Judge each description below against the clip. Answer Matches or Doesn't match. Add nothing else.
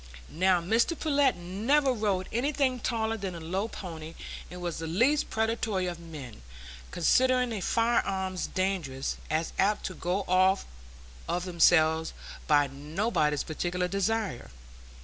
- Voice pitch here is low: Doesn't match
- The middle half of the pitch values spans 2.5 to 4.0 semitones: Doesn't match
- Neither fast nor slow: Doesn't match